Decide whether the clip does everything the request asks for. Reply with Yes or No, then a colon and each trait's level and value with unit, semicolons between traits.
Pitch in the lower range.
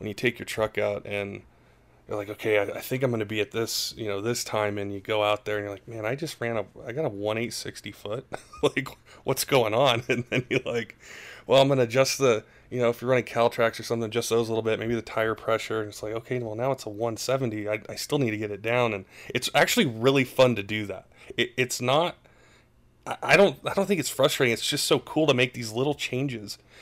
Yes: low, 115 Hz